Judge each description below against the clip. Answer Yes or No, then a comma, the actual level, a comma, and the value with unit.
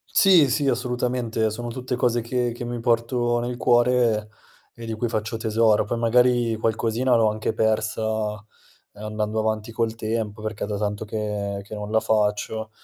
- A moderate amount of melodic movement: No, narrow, 1.9 semitones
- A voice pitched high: No, low, 115 Hz